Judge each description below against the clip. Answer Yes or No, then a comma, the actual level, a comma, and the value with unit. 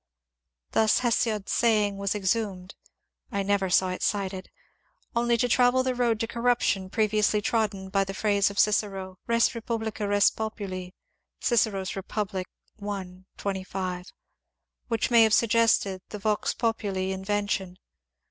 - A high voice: Yes, high, 205 Hz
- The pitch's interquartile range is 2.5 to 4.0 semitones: Yes, average, 2.8 semitones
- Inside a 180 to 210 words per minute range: No, average, 140 wpm